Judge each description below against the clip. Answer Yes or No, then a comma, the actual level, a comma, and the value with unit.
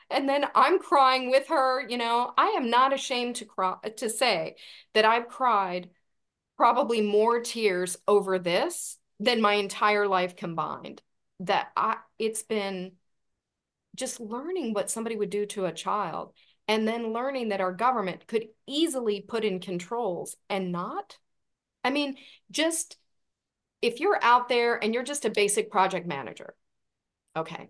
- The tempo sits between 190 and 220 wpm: No, average, 150 wpm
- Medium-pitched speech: No, high, 225 Hz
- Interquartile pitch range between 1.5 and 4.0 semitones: No, average, 4.4 semitones